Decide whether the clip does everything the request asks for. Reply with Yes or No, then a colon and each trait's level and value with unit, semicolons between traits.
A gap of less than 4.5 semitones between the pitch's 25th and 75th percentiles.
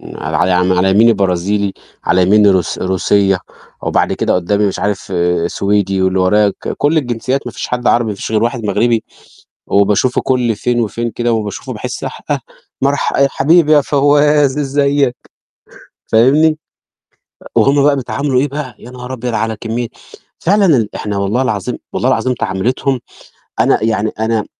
No: average, 4.8 semitones